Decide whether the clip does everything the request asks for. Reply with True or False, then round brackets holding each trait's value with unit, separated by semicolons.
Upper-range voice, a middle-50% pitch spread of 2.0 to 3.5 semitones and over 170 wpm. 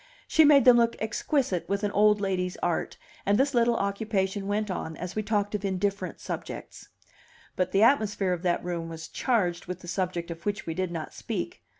True (200 Hz; 3.1 semitones; 200 wpm)